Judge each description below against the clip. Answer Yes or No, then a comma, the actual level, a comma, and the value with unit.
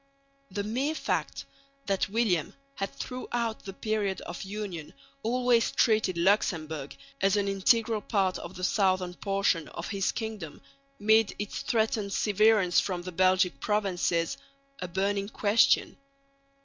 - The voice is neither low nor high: No, high, 200 Hz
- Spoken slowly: Yes, slow, 130 wpm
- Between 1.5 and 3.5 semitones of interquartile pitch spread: Yes, average, 3.0 semitones